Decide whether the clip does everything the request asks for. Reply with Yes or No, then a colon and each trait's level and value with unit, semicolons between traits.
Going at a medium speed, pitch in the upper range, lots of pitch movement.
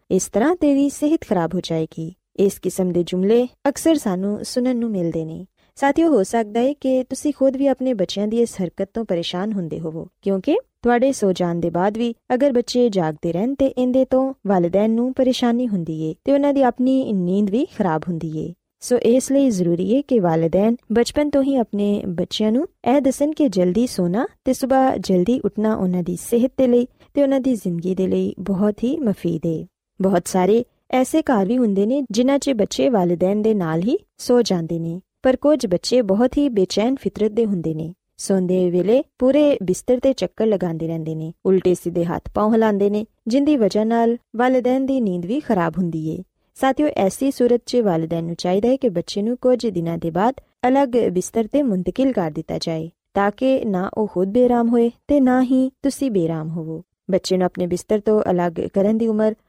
Yes: average, 135 wpm; high, 215 Hz; wide, 6.0 semitones